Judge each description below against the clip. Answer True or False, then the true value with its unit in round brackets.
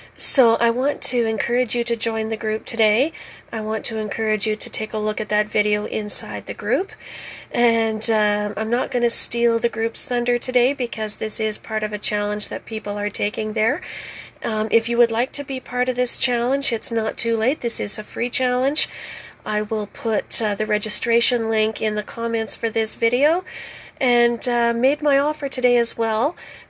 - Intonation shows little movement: True (2.2 semitones)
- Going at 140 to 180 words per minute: False (200 wpm)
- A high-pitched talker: True (230 Hz)